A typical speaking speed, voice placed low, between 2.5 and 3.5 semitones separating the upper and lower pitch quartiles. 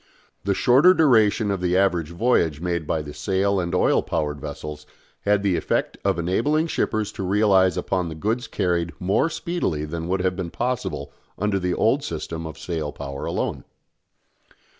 No: average, 170 wpm; very low, 95 Hz; average, 4.3 semitones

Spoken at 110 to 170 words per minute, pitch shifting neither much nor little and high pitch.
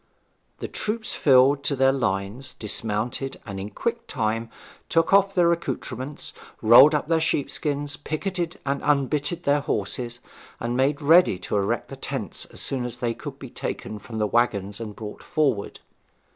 No: average, 165 wpm; average, 5.0 semitones; low, 135 Hz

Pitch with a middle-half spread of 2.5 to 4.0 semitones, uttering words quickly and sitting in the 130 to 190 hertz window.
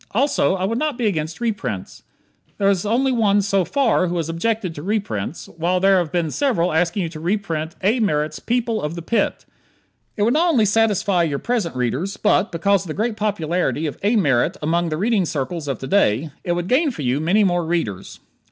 No: average, 5.0 semitones; fast, 210 wpm; medium, 185 Hz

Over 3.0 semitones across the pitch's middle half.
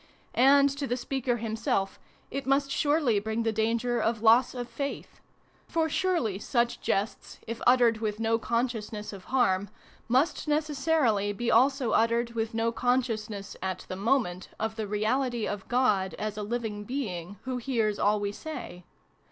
Yes: average, 3.5 semitones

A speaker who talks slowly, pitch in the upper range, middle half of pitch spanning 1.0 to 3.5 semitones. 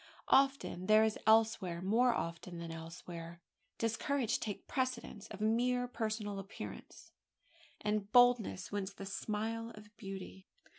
Yes: slow, 130 wpm; high, 215 Hz; average, 3.2 semitones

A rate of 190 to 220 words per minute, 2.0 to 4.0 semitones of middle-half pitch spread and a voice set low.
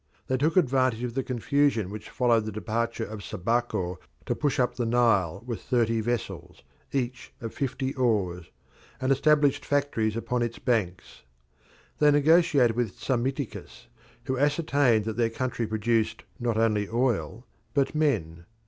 No: average, 145 wpm; average, 3.4 semitones; low, 120 Hz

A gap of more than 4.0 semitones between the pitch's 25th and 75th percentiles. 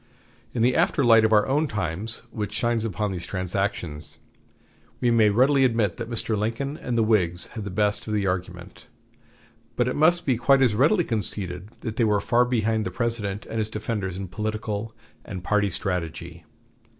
No: average, 3.5 semitones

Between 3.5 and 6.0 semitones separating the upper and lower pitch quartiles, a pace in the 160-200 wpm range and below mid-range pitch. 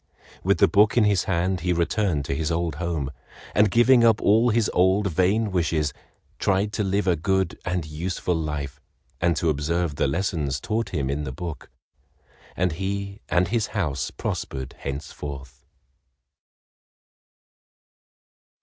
No: average, 4.8 semitones; average, 145 wpm; very low, 90 Hz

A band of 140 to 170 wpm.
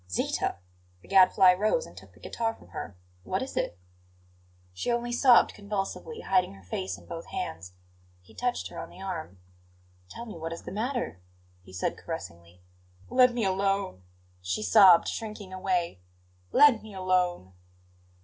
Yes: average, 160 wpm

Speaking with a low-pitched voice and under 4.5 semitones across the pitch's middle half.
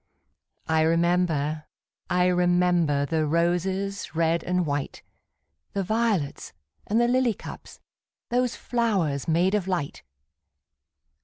No: medium, 175 Hz; average, 3.6 semitones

